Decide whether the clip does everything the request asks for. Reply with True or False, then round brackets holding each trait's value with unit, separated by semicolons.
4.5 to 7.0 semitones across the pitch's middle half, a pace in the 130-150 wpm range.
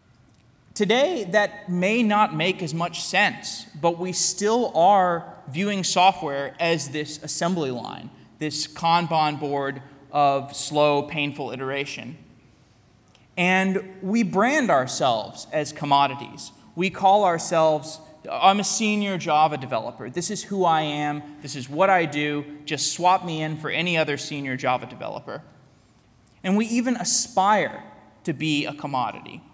True (4.9 semitones; 135 wpm)